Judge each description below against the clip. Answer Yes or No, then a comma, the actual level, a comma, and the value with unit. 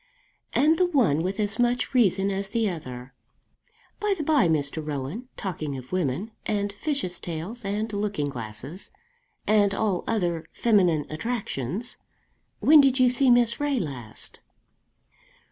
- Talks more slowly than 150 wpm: Yes, average, 140 wpm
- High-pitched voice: Yes, high, 200 Hz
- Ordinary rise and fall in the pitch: No, wide, 7.4 semitones